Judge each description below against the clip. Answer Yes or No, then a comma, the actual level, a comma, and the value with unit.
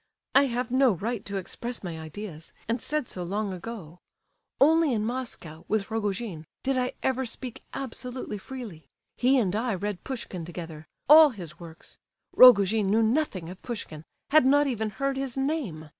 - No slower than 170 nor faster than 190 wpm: No, average, 160 wpm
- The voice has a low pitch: No, high, 220 Hz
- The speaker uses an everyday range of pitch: No, wide, 6.1 semitones